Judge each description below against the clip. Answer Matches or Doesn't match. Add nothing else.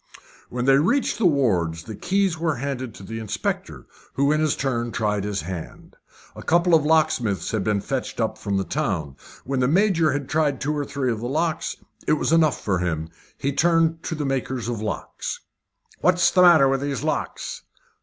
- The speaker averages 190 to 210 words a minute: Matches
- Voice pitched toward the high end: Doesn't match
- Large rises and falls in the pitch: Matches